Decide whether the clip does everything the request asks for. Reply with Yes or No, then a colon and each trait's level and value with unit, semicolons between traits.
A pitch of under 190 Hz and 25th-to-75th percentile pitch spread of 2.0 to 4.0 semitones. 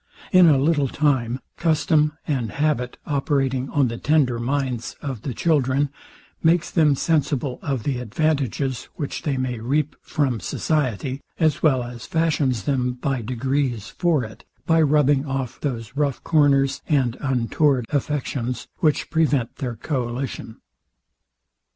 Yes: low, 135 Hz; average, 3.2 semitones